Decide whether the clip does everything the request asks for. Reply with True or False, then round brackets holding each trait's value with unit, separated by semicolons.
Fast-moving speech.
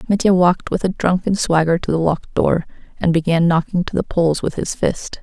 True (220 wpm)